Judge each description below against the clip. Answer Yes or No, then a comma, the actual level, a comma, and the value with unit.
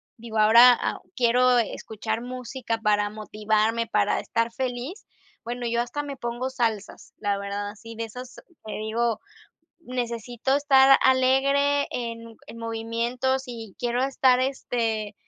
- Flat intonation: Yes, narrow, 2.3 semitones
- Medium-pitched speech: No, high, 235 Hz